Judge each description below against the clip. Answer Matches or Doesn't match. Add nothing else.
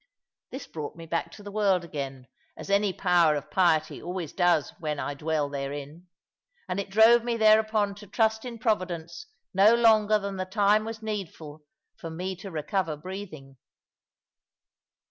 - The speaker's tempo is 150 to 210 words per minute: Matches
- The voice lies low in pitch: Doesn't match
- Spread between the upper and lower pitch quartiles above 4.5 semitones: Matches